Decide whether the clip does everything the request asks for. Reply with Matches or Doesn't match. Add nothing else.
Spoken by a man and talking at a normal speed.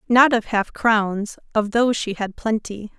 Doesn't match